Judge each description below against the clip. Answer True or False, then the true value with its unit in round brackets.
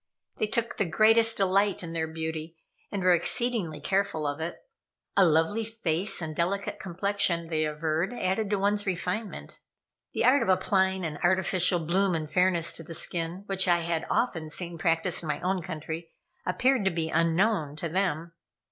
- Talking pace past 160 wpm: True (175 wpm)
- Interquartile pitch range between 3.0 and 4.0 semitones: True (3.5 semitones)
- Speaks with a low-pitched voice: False (175 Hz)